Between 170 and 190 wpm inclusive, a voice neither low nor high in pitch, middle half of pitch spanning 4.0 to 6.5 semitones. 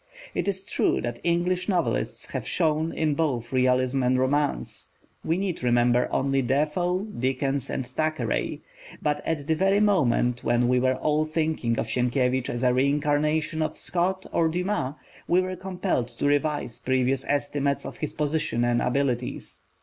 No: average, 155 wpm; medium, 145 Hz; average, 4.3 semitones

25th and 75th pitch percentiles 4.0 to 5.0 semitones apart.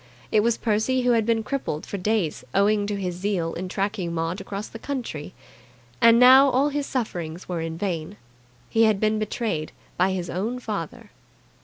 Yes: average, 4.4 semitones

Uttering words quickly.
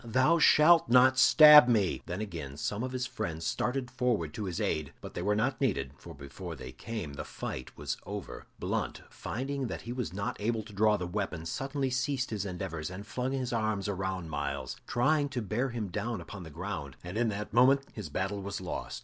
Yes: fast, 210 wpm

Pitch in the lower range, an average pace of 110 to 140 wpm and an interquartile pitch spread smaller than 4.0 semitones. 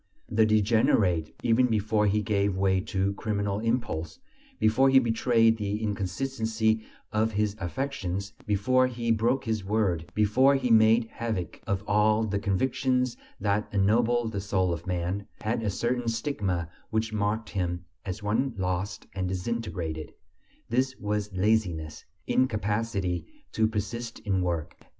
Yes: low, 105 Hz; slow, 135 wpm; average, 3.0 semitones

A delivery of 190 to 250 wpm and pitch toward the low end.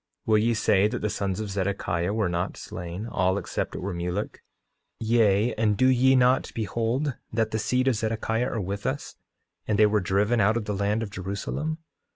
Yes: average, 195 wpm; low, 105 Hz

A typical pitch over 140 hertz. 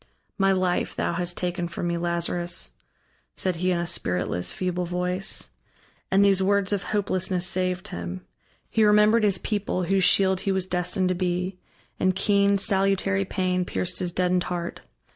Yes: medium, 185 Hz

